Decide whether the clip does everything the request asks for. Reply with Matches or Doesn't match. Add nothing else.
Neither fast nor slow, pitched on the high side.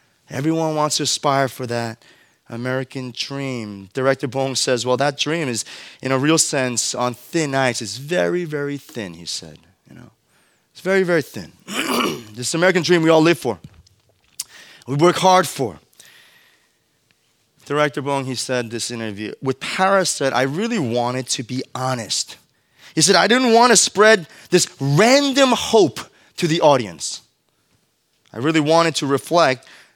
Doesn't match